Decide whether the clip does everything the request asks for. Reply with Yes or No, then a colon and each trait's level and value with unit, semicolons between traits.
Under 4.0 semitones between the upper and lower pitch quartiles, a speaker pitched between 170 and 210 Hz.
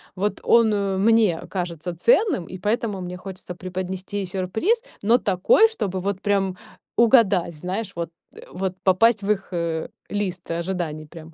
Yes: average, 2.8 semitones; high, 190 Hz